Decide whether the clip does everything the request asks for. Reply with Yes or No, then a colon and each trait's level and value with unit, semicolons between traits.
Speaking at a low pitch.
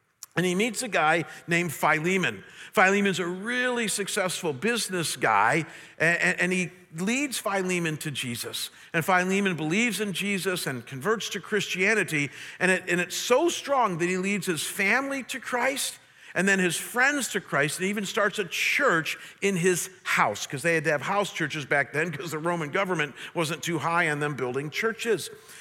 No: medium, 180 Hz